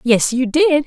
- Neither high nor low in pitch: No, very high, 275 Hz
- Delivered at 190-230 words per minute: Yes, fast, 210 wpm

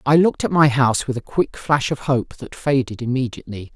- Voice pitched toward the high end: No, low, 130 Hz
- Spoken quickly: Yes, fast, 225 wpm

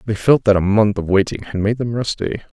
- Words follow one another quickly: Yes, fast, 255 wpm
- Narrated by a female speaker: No, male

